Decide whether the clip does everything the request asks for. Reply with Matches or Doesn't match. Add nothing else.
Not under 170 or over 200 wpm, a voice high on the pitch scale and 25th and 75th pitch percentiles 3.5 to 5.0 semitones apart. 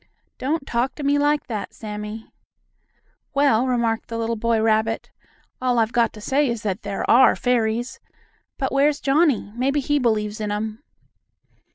Doesn't match